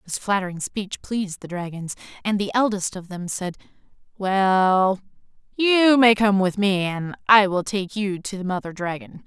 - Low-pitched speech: No, high, 195 Hz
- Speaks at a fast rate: No, average, 175 wpm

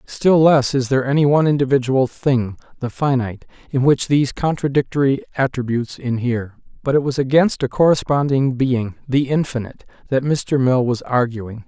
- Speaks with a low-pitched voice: Yes, low, 130 Hz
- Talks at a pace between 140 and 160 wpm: Yes, average, 155 wpm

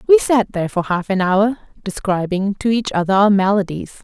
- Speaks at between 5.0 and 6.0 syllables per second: Yes, 5.2 syllables/s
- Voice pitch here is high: Yes, high, 205 Hz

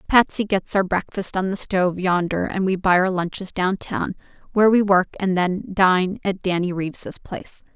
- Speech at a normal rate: Yes, average, 195 wpm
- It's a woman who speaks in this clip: Yes, female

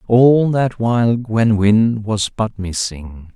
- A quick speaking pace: No, average, 145 wpm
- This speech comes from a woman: No, male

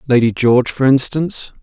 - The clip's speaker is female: No, male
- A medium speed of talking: Yes, average, 150 wpm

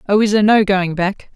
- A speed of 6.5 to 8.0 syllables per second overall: No, 6.0 syllables/s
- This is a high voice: Yes, high, 200 Hz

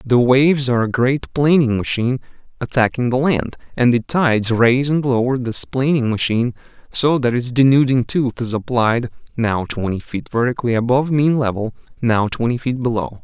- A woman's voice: No, male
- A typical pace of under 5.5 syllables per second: Yes, 5.3 syllables/s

